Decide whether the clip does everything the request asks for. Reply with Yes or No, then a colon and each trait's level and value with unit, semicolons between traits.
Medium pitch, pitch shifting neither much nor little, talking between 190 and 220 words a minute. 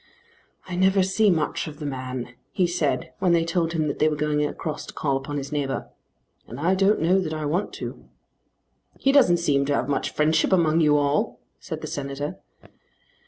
Yes: medium, 155 Hz; average, 3.5 semitones; average, 200 wpm